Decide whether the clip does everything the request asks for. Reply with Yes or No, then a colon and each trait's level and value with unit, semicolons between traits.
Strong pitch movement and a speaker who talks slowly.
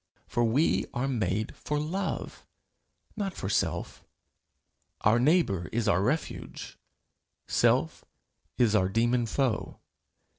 Yes: wide, 5.9 semitones; slow, 110 wpm